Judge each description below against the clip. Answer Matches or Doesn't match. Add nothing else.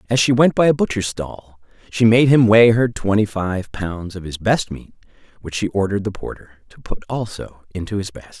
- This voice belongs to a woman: Doesn't match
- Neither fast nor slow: Doesn't match